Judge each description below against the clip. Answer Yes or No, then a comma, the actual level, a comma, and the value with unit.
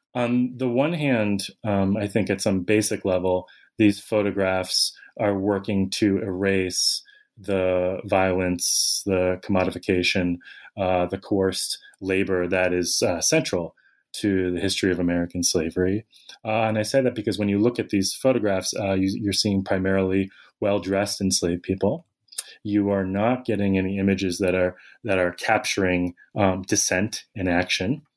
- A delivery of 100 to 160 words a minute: Yes, average, 150 wpm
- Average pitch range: No, narrow, 1.9 semitones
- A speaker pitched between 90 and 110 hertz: Yes, very low, 95 Hz